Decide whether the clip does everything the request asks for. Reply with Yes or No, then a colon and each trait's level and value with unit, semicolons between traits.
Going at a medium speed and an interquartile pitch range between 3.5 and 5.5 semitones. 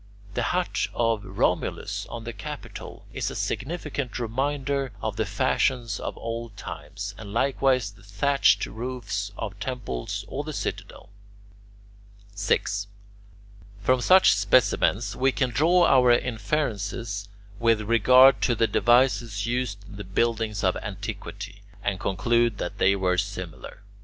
No: slow, 130 wpm; average, 4.0 semitones